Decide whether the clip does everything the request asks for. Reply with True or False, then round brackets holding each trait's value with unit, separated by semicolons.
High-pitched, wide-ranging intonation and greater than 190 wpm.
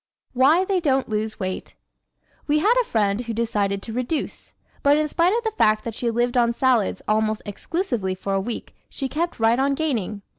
True (240 Hz; 5.8 semitones; 200 wpm)